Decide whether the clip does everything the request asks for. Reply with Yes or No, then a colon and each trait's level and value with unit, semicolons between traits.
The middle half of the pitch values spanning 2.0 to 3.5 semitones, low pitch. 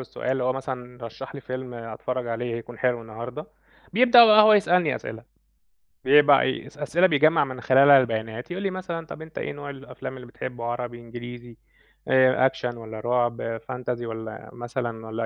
Yes: average, 3.2 semitones; low, 125 Hz